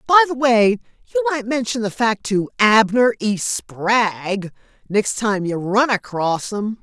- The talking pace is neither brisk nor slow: Yes, average, 160 wpm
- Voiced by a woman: Yes, female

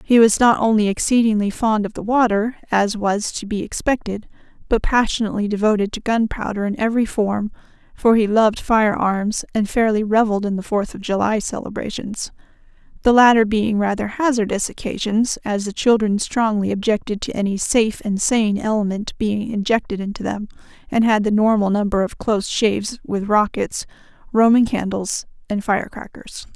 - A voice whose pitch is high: Yes, high, 215 Hz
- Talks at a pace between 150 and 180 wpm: Yes, average, 155 wpm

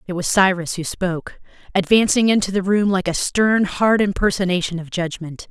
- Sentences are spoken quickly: No, average, 175 wpm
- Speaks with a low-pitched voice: No, high, 190 Hz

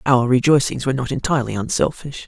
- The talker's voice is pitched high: No, low, 130 Hz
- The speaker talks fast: No, average, 160 wpm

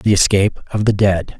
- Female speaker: No, male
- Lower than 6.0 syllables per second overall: Yes, 5.7 syllables/s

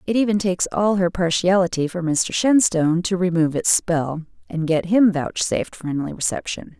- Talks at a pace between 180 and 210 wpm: No, average, 170 wpm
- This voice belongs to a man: No, female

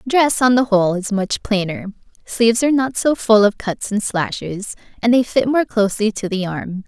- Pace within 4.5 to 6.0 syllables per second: Yes, 5.1 syllables/s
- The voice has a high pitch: Yes, high, 220 Hz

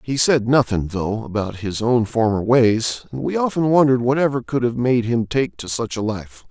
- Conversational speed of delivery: No, fast, 210 wpm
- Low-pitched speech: Yes, low, 120 Hz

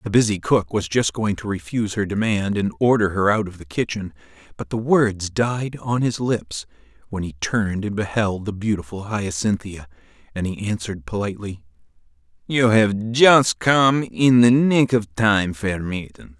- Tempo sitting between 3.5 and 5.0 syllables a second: Yes, 4.6 syllables/s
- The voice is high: No, low, 105 Hz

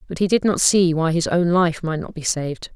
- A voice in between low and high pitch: Yes, medium, 170 Hz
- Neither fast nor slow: No, fast, 285 wpm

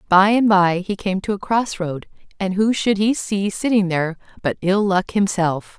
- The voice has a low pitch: No, high, 195 Hz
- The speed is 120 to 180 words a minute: No, fast, 205 wpm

